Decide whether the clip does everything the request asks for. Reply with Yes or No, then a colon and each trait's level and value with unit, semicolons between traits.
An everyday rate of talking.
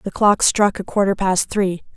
No: fast, 215 wpm